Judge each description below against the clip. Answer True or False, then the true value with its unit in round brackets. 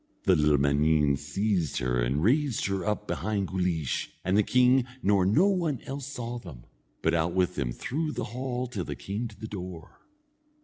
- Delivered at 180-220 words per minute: True (185 wpm)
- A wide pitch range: True (7.5 semitones)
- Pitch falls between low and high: False (95 Hz)